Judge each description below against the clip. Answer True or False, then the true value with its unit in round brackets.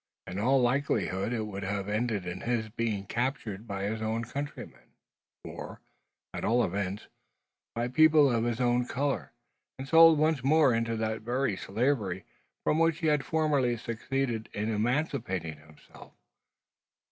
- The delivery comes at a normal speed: True (145 wpm)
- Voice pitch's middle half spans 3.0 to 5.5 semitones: True (4.7 semitones)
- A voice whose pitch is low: True (115 Hz)